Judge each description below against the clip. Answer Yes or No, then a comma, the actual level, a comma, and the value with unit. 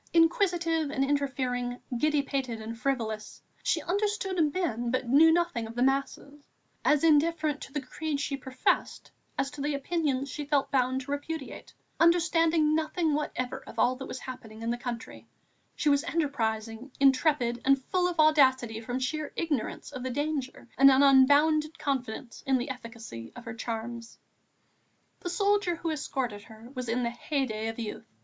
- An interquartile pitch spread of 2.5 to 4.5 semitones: Yes, average, 4.0 semitones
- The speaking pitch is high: Yes, very high, 275 Hz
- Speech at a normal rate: Yes, average, 165 wpm